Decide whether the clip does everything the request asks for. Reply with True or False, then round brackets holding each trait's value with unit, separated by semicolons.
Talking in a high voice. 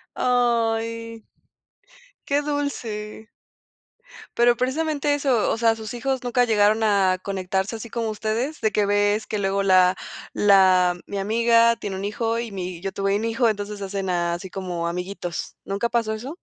True (215 Hz)